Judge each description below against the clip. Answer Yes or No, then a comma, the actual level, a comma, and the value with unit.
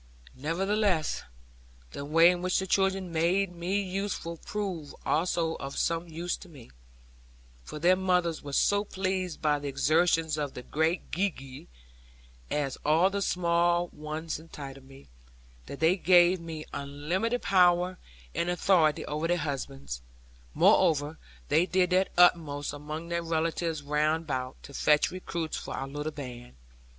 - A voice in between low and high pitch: Yes, medium, 165 Hz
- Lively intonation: No, average, 3.4 semitones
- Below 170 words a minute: Yes, average, 145 wpm